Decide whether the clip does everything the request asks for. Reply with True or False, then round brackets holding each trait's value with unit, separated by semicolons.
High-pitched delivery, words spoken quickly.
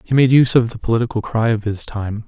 False (115 Hz; 265 wpm)